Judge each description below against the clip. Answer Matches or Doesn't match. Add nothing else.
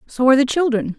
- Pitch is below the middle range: Doesn't match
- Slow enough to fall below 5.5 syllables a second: Doesn't match